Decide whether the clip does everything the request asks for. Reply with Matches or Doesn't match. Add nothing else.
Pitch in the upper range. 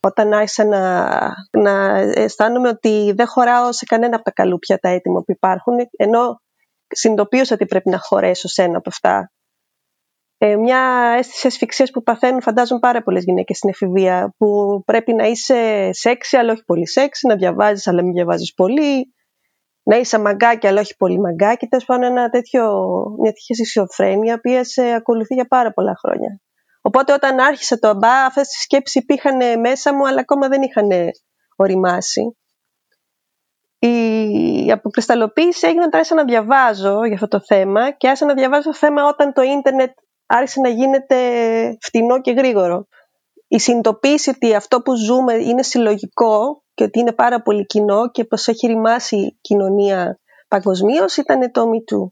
Matches